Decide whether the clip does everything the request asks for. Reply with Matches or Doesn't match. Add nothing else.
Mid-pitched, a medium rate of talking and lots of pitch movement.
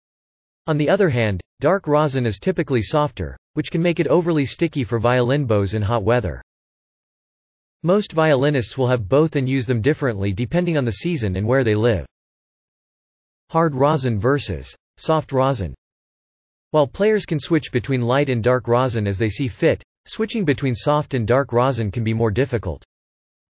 Doesn't match